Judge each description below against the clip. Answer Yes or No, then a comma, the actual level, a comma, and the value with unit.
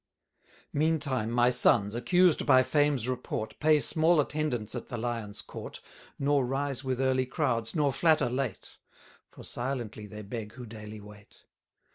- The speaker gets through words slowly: No, average, 145 wpm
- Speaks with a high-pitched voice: No, low, 130 Hz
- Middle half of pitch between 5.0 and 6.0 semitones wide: No, average, 4.2 semitones